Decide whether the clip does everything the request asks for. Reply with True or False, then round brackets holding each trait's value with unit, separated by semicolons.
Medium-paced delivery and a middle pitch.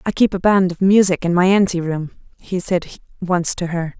False (225 wpm; 180 Hz)